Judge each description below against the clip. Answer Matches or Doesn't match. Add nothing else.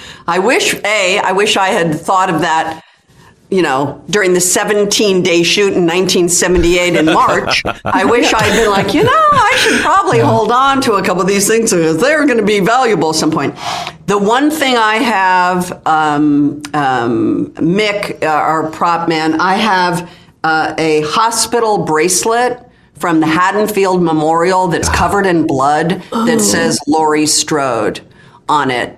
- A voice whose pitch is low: Doesn't match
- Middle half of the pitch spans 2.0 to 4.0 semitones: Doesn't match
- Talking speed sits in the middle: Matches